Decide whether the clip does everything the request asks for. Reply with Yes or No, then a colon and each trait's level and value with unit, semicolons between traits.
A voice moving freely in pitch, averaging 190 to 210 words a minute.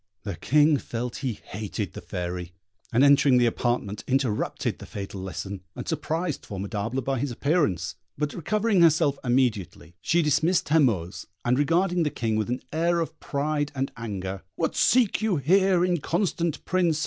No: wide, 7.2 semitones; average, 160 wpm